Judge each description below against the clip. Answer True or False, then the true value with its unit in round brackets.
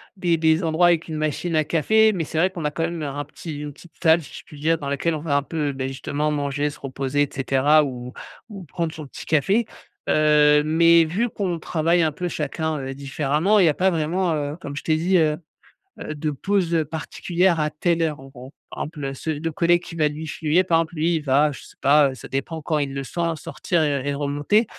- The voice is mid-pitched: True (155 Hz)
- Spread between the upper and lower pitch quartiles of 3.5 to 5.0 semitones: False (2.6 semitones)